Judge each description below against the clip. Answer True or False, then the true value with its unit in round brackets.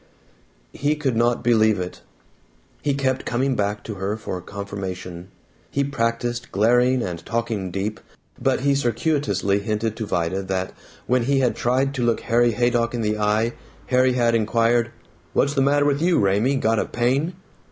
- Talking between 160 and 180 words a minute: True (165 wpm)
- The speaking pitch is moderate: False (115 Hz)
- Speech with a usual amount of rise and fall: True (3.9 semitones)